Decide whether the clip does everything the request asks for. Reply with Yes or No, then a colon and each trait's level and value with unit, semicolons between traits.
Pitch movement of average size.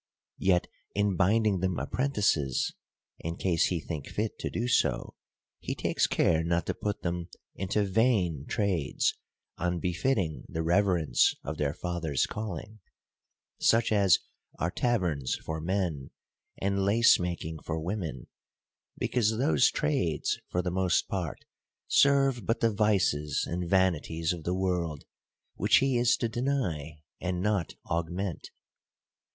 Yes: average, 4.4 semitones